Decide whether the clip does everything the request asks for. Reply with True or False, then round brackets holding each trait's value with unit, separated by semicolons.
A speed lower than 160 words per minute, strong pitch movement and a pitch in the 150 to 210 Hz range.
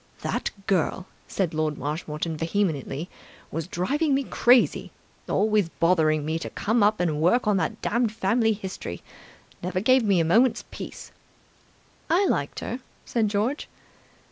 True (140 wpm; 5.9 semitones; 190 Hz)